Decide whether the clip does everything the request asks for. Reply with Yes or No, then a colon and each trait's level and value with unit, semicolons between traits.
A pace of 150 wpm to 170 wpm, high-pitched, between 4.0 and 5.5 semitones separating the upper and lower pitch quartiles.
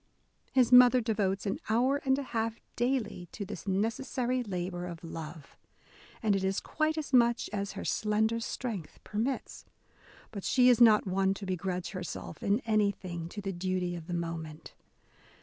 Yes: average, 165 wpm; high, 205 Hz; average, 4.7 semitones